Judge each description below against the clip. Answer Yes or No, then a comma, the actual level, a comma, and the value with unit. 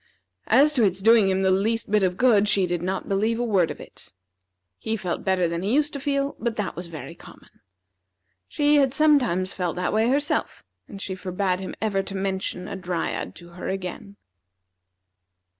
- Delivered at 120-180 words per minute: No, average, 190 wpm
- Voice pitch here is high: Yes, high, 195 Hz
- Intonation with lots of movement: No, average, 3.9 semitones